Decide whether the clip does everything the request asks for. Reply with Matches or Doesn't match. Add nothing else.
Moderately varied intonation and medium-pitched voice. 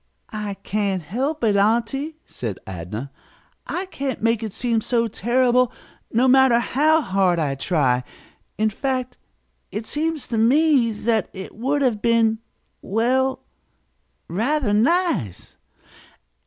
Doesn't match